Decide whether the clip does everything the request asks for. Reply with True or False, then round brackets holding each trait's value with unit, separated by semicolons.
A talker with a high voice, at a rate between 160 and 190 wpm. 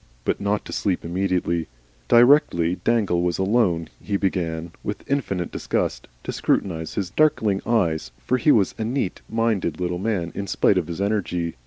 False (95 Hz; 165 wpm)